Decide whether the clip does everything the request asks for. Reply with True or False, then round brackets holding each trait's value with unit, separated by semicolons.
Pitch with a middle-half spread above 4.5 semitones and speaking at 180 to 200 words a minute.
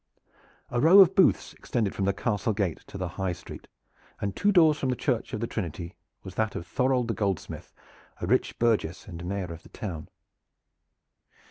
True (5.1 semitones; 190 wpm)